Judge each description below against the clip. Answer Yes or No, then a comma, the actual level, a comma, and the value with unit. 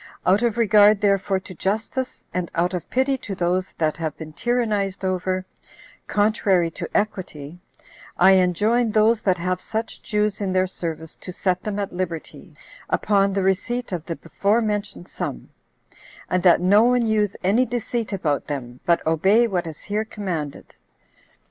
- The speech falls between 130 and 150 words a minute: No, average, 160 wpm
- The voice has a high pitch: Yes, high, 195 Hz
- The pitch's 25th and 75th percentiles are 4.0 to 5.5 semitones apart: No, average, 3.3 semitones